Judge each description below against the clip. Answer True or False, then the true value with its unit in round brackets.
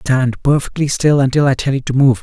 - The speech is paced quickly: True (245 wpm)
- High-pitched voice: False (130 Hz)